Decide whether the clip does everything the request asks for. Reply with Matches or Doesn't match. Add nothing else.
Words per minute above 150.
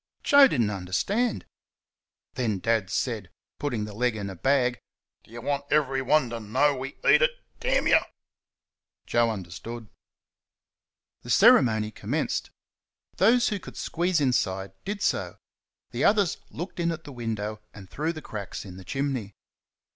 Doesn't match